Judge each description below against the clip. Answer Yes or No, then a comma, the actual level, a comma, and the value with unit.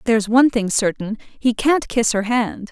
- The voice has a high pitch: Yes, high, 230 Hz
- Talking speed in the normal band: Yes, average, 175 wpm